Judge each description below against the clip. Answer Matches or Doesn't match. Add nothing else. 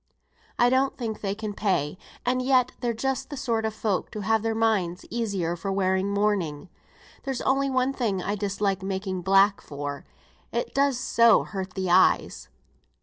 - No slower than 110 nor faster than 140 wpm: Doesn't match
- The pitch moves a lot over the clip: Doesn't match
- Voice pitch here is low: Doesn't match